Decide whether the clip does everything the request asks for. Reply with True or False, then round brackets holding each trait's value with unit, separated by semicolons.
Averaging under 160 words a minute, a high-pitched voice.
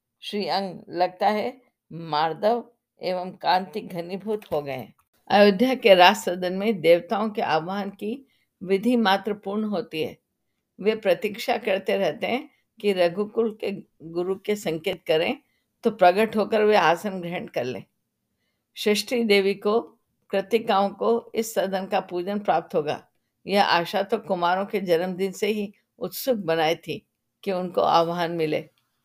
True (145 wpm; 200 Hz)